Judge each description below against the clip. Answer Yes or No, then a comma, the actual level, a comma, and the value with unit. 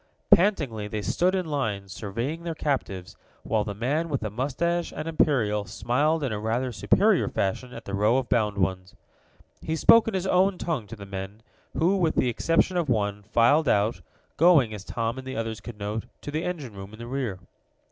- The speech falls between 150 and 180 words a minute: No, average, 200 wpm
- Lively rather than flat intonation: Yes, wide, 7.1 semitones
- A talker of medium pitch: No, low, 120 Hz